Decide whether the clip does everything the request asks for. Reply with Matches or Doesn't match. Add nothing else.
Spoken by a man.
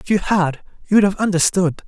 Matches